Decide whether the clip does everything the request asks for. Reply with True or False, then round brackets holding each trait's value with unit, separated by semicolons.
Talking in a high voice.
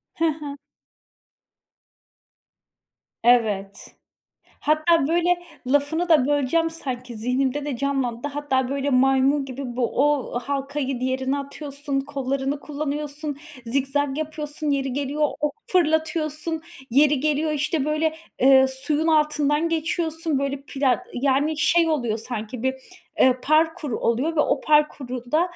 True (285 Hz)